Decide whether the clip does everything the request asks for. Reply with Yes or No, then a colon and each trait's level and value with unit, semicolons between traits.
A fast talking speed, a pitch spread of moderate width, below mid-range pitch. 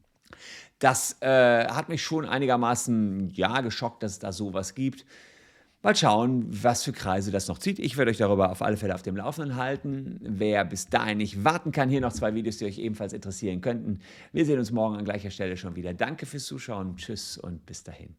Yes: fast, 210 wpm; average, 5.0 semitones; low, 110 Hz